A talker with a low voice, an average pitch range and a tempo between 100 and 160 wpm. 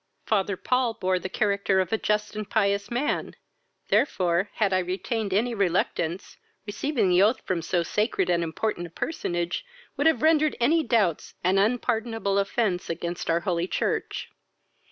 No: high, 200 Hz; average, 4.0 semitones; average, 155 wpm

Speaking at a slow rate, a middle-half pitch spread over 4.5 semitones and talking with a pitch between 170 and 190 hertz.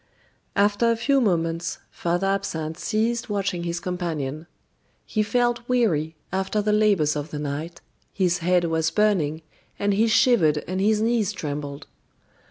No: average, 145 wpm; average, 4.9 semitones; medium, 185 Hz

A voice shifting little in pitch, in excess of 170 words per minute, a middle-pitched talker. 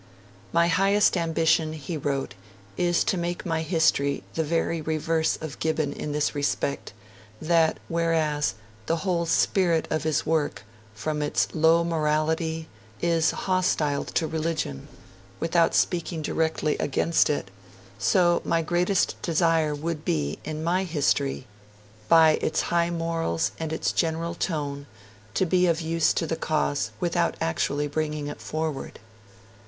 No: narrow, 1.8 semitones; slow, 135 wpm; medium, 160 Hz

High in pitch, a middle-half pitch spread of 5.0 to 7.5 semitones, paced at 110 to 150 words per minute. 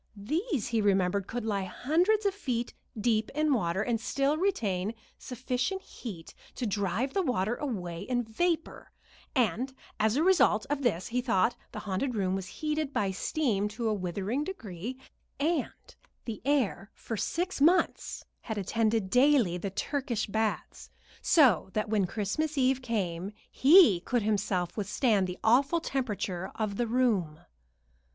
Yes: high, 225 Hz; wide, 5.6 semitones; average, 145 wpm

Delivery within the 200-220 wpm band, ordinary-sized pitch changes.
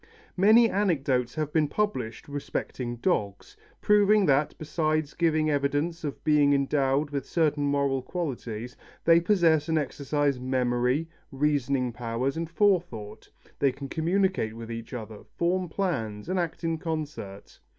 No: slow, 135 wpm; average, 4.7 semitones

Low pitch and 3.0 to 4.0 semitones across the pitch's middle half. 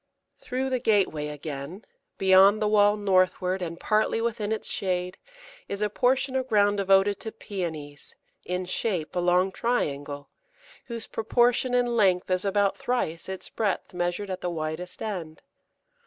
No: high, 195 Hz; average, 3.4 semitones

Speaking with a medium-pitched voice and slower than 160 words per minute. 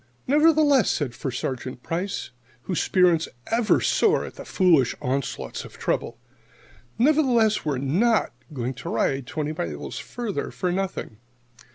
Yes: medium, 175 Hz; slow, 135 wpm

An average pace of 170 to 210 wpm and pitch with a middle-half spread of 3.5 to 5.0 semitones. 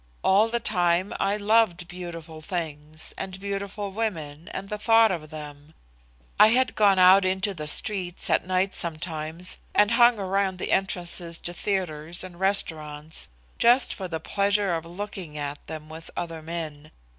No: average, 155 wpm; average, 3.8 semitones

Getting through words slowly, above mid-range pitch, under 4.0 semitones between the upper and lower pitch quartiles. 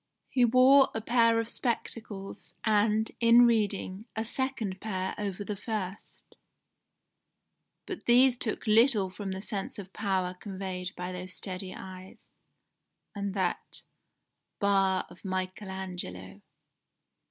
Yes: slow, 120 wpm; high, 200 Hz; average, 3.3 semitones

